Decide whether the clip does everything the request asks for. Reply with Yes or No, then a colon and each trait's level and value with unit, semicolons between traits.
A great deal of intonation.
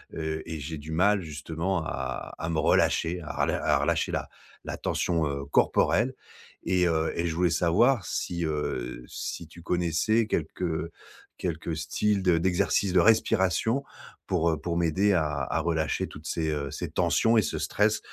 No: average, 2.7 semitones